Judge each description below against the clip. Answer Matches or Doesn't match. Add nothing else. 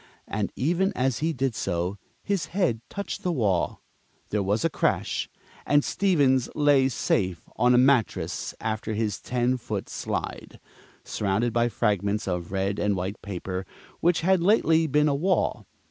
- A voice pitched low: Matches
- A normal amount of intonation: Doesn't match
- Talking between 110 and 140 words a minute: Doesn't match